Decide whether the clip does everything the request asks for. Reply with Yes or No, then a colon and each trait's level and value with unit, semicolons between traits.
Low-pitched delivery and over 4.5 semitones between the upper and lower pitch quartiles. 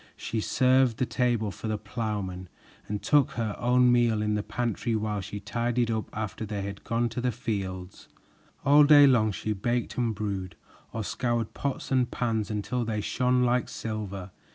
No: low, 110 Hz; average, 2.8 semitones